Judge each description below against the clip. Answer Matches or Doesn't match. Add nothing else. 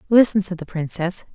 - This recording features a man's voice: Doesn't match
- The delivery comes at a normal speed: Matches